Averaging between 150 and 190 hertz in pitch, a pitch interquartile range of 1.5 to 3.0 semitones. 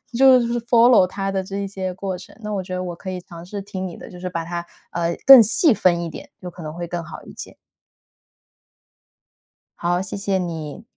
Yes: medium, 185 Hz; average, 2.7 semitones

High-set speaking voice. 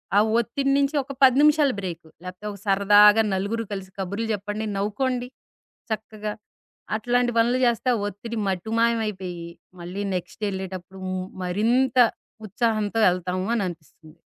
Yes: high, 210 Hz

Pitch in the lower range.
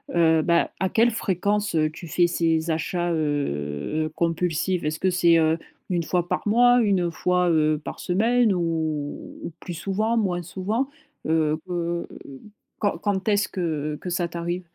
No: medium, 175 Hz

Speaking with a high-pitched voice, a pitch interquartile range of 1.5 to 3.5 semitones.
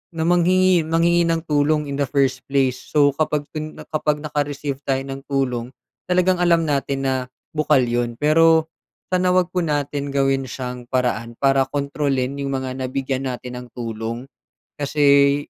No: medium, 140 Hz; average, 2.8 semitones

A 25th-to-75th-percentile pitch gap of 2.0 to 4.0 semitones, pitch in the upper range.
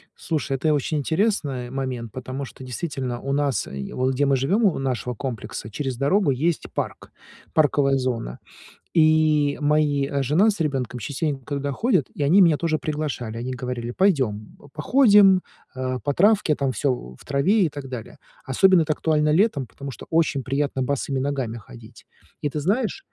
No: average, 3.5 semitones; medium, 140 Hz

